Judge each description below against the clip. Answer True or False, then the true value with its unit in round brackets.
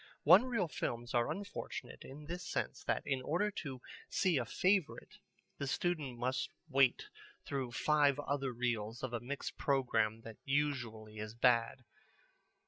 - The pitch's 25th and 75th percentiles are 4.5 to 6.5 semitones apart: False (4.0 semitones)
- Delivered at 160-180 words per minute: False (145 wpm)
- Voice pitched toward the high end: False (135 Hz)